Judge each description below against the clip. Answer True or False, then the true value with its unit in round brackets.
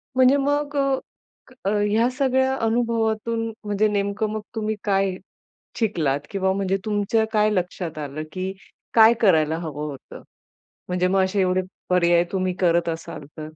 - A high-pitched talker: True (200 Hz)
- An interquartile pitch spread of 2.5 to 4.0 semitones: True (3.7 semitones)